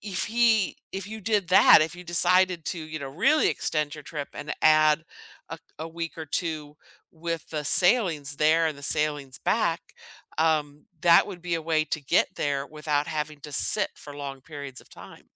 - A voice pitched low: No, medium, 155 Hz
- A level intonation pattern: No, average, 3.0 semitones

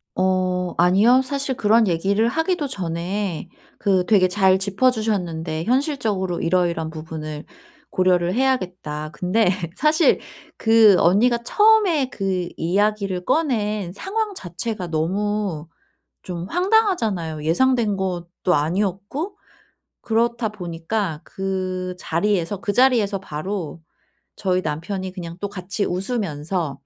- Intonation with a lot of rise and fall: No, average, 4.4 semitones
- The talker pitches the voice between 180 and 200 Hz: Yes, high, 195 Hz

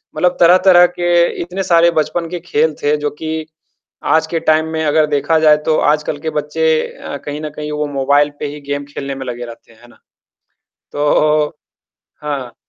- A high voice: No, medium, 150 Hz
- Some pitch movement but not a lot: No, narrow, 1.9 semitones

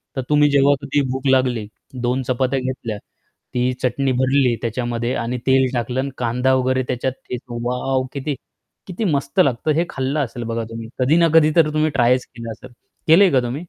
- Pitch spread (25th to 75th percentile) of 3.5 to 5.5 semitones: No, narrow, 2.4 semitones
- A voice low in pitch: Yes, low, 130 Hz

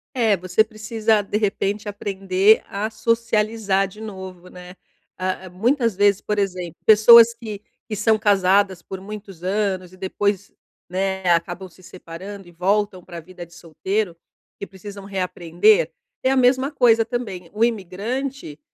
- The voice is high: Yes, high, 200 Hz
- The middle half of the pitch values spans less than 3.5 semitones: Yes, average, 2.8 semitones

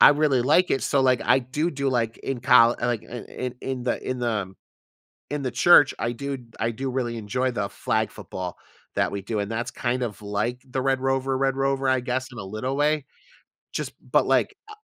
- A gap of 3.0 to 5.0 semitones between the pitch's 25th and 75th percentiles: No, narrow, 2.6 semitones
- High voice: No, low, 125 Hz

